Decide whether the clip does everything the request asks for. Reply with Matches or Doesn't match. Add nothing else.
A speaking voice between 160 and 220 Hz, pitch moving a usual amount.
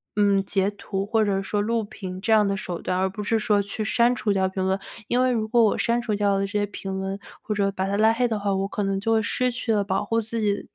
Doesn't match